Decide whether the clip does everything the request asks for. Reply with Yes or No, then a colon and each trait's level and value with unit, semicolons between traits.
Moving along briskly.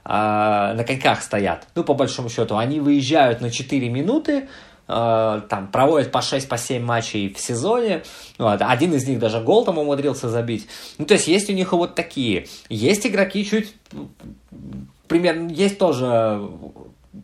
No: average, 150 wpm